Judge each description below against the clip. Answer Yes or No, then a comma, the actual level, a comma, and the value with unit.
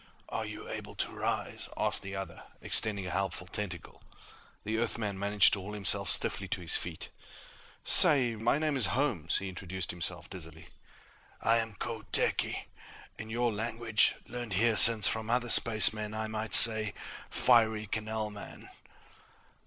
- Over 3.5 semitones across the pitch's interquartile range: No, average, 2.8 semitones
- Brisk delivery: No, average, 150 wpm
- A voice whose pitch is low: Yes, low, 110 Hz